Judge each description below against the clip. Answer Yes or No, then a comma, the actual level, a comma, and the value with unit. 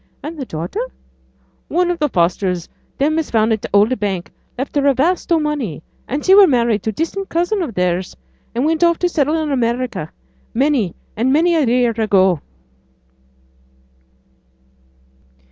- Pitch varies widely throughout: Yes, wide, 7.3 semitones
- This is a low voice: No, very high, 260 Hz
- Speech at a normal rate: Yes, average, 160 wpm